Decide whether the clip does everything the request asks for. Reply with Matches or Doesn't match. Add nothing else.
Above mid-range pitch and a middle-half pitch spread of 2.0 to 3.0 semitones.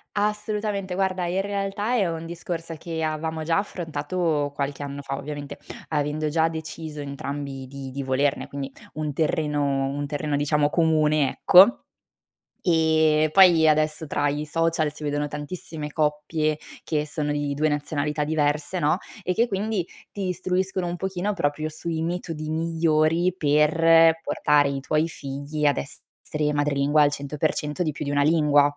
Doesn't match